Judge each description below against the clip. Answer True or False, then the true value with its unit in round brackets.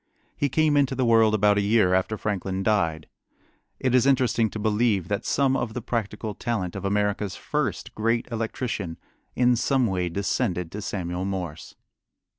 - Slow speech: False (165 wpm)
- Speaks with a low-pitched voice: True (105 Hz)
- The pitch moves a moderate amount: True (3.7 semitones)